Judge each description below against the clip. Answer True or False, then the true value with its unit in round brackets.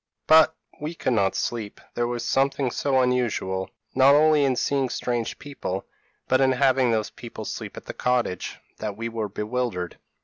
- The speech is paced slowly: False (175 wpm)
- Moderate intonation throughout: True (3.4 semitones)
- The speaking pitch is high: False (125 Hz)